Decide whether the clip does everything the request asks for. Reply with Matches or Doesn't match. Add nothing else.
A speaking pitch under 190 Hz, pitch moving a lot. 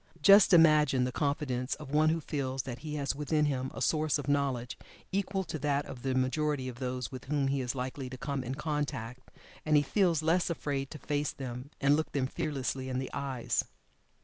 Doesn't match